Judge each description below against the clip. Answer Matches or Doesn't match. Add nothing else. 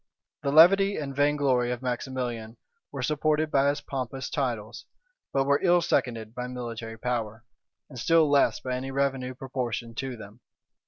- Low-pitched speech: Matches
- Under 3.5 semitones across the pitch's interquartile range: Matches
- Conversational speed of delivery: Matches